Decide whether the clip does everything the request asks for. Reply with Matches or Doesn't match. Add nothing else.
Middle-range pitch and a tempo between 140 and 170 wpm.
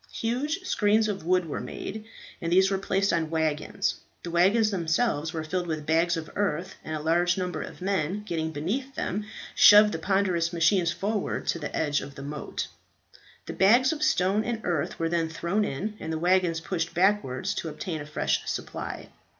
Doesn't match